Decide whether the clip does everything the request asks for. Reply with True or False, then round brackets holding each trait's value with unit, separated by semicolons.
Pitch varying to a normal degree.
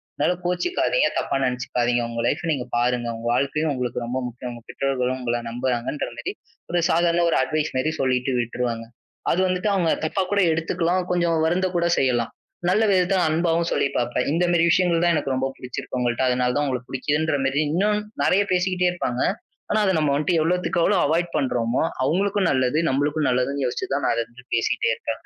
False (5.7 semitones)